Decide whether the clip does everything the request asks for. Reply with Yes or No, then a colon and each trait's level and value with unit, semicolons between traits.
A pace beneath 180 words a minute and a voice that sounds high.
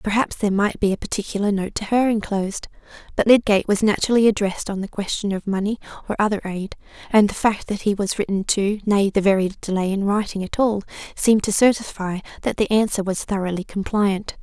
No: average, 200 wpm; high, 205 Hz